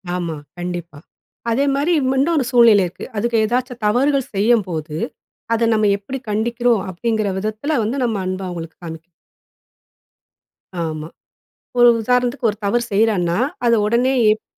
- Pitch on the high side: Yes, high, 220 Hz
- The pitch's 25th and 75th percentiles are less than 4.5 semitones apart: No, average, 4.8 semitones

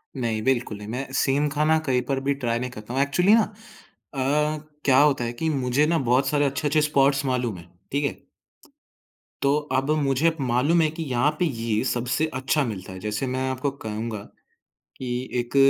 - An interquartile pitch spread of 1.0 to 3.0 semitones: No, average, 3.4 semitones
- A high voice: No, low, 135 Hz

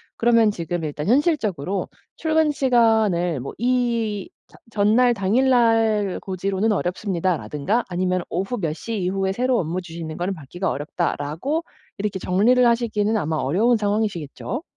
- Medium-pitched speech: No, high, 205 Hz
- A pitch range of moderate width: Yes, average, 4.9 semitones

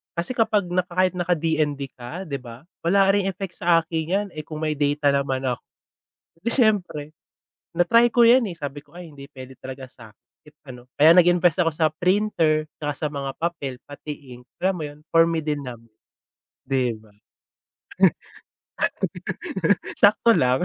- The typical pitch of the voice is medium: Yes, medium, 155 Hz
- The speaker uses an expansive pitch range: No, average, 4.3 semitones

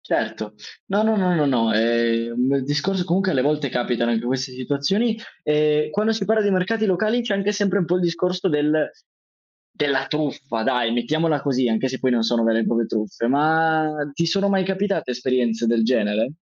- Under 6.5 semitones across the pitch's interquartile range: No, wide, 7.2 semitones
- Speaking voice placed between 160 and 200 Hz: No, medium, 145 Hz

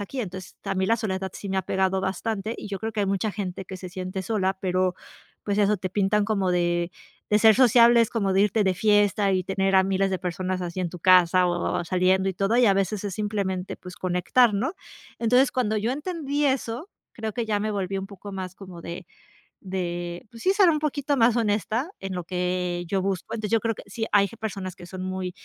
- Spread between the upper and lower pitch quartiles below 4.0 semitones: Yes, average, 2.9 semitones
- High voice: Yes, high, 195 Hz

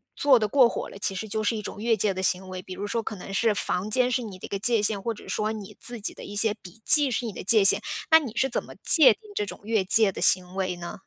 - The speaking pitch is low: No, high, 210 Hz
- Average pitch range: Yes, average, 3.0 semitones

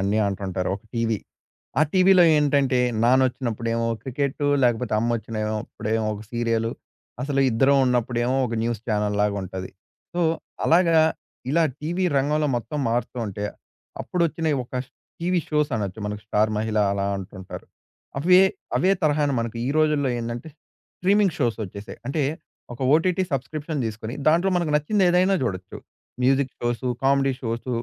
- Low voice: Yes, low, 125 Hz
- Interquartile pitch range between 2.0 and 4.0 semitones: No, wide, 5.4 semitones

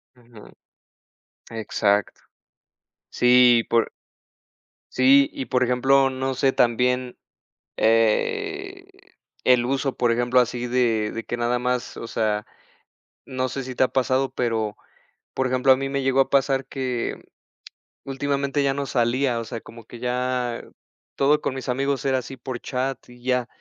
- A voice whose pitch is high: No, low, 125 Hz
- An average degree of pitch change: No, narrow, 2.0 semitones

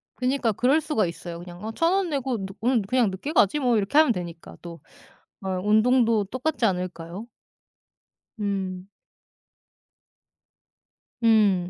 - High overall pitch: Yes, high, 215 Hz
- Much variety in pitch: Yes, wide, 5.7 semitones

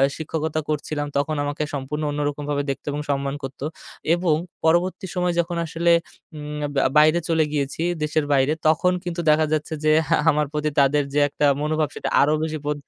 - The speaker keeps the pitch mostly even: Yes, narrow, 1.6 semitones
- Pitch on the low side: No, medium, 150 Hz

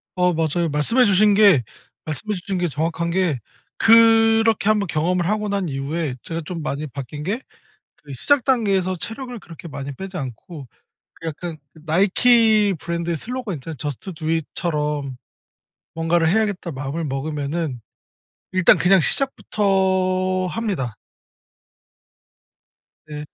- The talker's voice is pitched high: No, medium, 175 Hz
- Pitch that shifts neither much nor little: Yes, average, 4.9 semitones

